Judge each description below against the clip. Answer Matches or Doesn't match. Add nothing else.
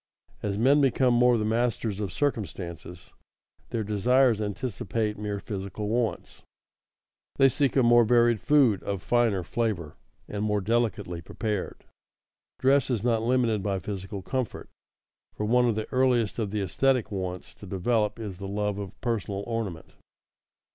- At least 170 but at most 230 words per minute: Doesn't match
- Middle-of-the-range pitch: Doesn't match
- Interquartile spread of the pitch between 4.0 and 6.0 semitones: Doesn't match